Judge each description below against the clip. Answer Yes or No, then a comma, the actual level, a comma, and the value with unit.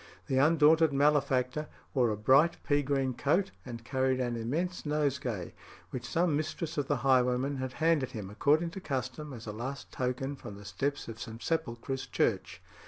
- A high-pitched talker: No, low, 135 Hz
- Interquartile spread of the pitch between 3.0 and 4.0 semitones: Yes, average, 3.4 semitones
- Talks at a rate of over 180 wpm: No, average, 170 wpm